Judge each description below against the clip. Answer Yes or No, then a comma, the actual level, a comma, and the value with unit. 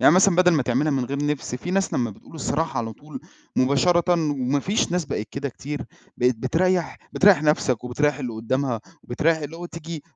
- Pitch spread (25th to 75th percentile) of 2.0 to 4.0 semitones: No, average, 4.6 semitones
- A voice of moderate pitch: Yes, medium, 145 Hz